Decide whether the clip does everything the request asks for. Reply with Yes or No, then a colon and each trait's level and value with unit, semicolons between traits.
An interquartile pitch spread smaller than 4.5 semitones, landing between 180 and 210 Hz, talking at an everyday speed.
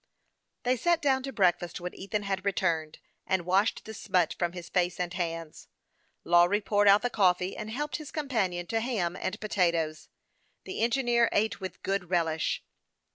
Yes: average, 4.1 semitones; high, 190 Hz; average, 180 wpm